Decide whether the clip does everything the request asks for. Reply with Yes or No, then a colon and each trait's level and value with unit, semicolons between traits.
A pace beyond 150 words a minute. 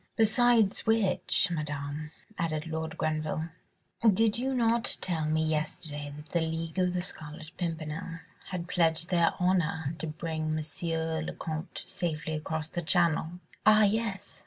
No: average, 140 wpm